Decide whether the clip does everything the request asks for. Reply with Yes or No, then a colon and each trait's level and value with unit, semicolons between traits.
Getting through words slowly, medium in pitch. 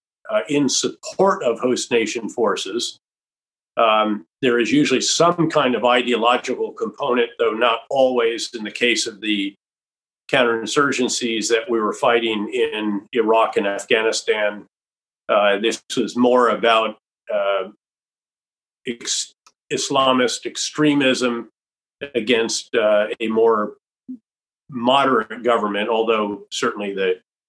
No: slow, 110 wpm; low, 120 Hz